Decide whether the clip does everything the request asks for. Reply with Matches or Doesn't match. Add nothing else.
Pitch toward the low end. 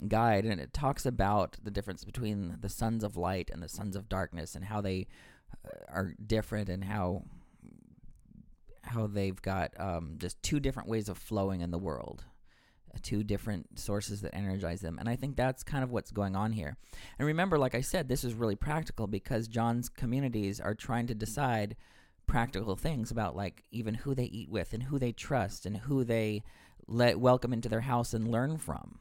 Matches